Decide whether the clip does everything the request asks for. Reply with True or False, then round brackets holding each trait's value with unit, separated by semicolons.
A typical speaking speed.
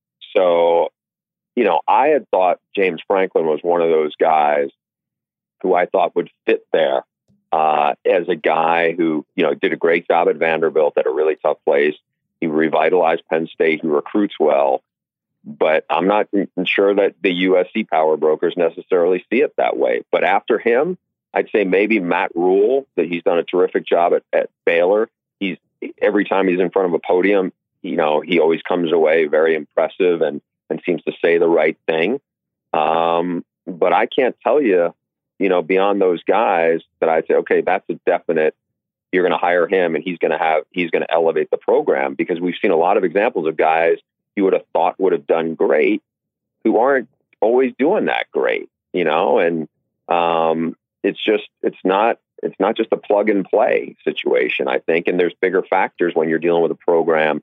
True (195 wpm)